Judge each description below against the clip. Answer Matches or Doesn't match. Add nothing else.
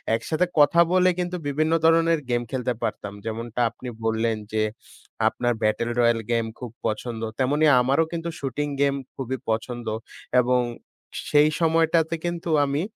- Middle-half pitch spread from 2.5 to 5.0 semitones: Doesn't match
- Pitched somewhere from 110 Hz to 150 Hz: Matches